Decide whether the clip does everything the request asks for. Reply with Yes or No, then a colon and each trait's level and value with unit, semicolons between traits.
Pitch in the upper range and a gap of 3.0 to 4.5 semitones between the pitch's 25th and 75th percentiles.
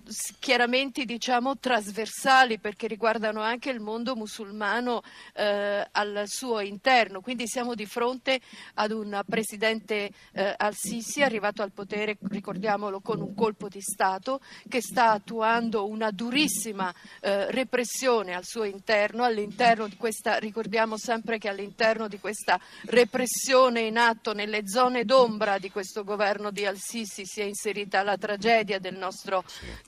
No: high, 220 Hz; narrow, 2.5 semitones